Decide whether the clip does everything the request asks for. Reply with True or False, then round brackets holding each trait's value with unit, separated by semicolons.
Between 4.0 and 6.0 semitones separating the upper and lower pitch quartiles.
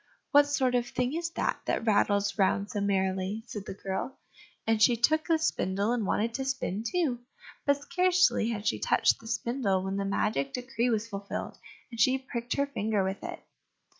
True (4.8 semitones)